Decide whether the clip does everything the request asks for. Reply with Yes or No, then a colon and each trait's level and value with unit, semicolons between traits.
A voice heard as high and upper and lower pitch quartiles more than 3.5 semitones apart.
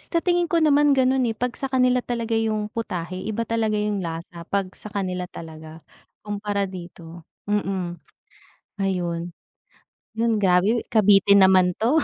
Yes: high, 205 Hz; average, 4.2 semitones